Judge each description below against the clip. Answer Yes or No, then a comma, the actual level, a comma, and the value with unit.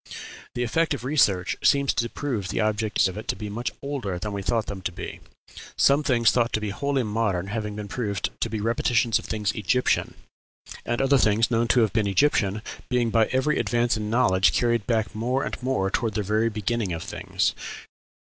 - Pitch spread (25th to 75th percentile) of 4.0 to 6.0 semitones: No, average, 2.9 semitones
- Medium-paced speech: No, fast, 210 wpm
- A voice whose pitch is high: No, low, 110 Hz